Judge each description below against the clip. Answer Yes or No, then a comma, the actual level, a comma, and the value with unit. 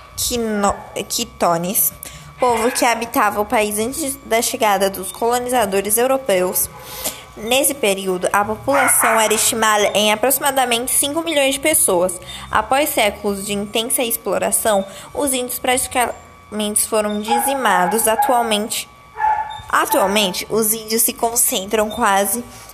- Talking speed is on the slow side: Yes, slow, 110 wpm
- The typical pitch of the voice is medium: No, high, 225 Hz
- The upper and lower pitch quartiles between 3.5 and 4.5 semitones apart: Yes, average, 3.9 semitones